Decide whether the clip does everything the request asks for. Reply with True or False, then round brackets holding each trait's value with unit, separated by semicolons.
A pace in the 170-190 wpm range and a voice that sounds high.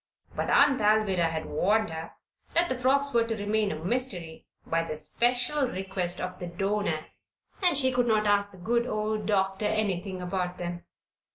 True (175 wpm; 205 Hz)